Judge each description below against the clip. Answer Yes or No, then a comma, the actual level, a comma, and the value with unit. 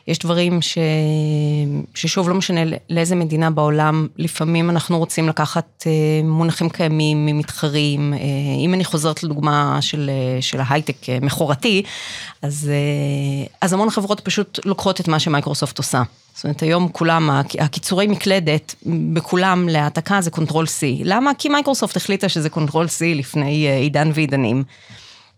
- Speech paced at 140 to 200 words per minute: No, average, 130 wpm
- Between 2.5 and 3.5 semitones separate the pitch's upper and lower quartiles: Yes, average, 2.9 semitones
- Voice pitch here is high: No, medium, 155 Hz